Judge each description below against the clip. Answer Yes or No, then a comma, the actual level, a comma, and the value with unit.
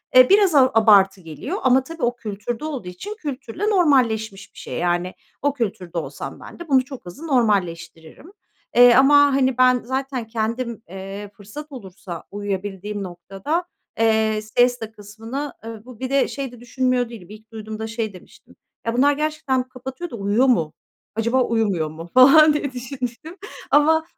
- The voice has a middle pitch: No, high, 235 Hz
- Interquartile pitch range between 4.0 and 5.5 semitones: Yes, average, 4.8 semitones